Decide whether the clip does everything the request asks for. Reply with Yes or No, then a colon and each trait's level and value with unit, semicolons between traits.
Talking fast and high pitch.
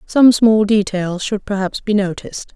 No: average, 165 wpm; high, 205 Hz